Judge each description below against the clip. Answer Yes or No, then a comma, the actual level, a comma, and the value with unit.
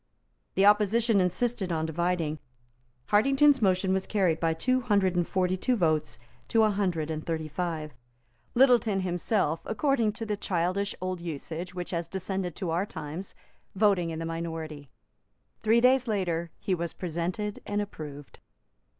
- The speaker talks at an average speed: Yes, average, 150 wpm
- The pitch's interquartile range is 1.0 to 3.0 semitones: No, average, 4.0 semitones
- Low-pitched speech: No, medium, 185 Hz